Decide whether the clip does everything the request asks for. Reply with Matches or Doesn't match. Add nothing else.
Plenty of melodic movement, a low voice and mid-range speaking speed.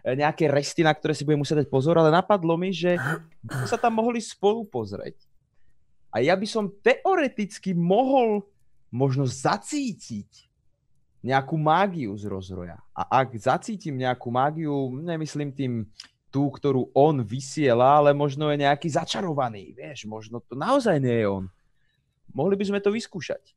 Doesn't match